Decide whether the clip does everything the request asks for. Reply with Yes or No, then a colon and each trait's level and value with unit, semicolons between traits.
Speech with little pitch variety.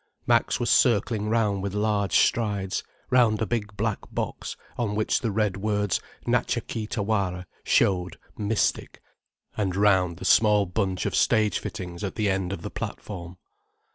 Yes: narrow, 2.2 semitones